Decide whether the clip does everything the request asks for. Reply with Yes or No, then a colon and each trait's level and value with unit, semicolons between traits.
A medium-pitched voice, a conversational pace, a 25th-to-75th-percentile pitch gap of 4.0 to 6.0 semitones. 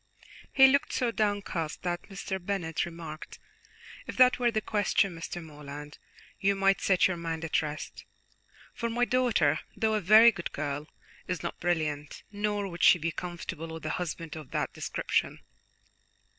Yes: medium, 175 Hz; average, 160 wpm; average, 4.5 semitones